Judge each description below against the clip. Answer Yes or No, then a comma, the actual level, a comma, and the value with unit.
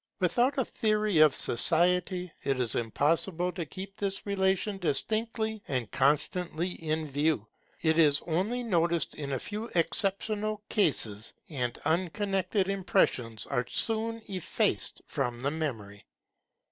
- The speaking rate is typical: No, slow, 125 wpm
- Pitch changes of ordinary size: No, wide, 5.8 semitones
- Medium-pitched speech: Yes, medium, 175 Hz